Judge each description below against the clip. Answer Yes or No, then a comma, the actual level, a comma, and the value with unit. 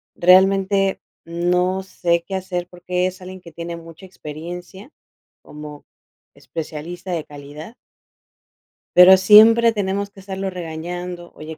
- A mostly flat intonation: Yes, narrow, 2.2 semitones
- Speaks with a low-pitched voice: No, medium, 180 Hz